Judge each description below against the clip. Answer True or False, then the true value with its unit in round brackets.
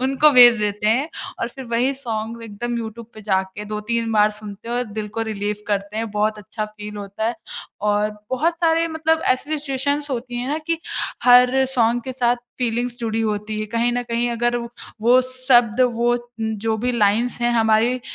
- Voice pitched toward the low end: False (235 Hz)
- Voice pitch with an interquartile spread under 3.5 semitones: True (2.8 semitones)